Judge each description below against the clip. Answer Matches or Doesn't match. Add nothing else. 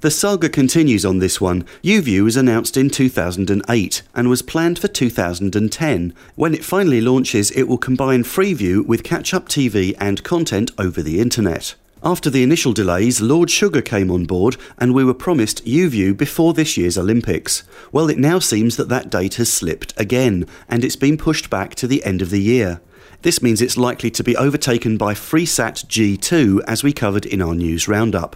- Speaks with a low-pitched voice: Matches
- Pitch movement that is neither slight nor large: Doesn't match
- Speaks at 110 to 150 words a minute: Doesn't match